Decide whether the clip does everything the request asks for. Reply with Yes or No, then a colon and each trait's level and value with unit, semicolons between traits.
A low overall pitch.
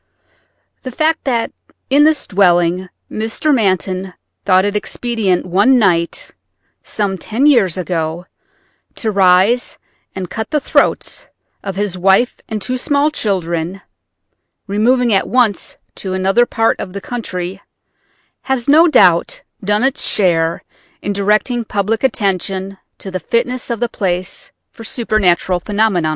No: high, 205 Hz